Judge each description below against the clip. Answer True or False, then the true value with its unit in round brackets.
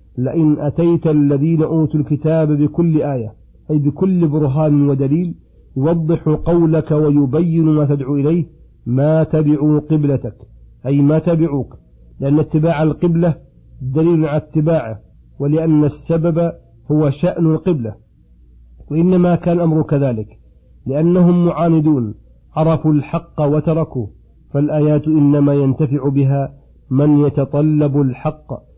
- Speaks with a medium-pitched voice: True (150 Hz)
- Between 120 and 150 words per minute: False (105 wpm)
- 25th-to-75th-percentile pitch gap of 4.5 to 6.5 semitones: False (2.5 semitones)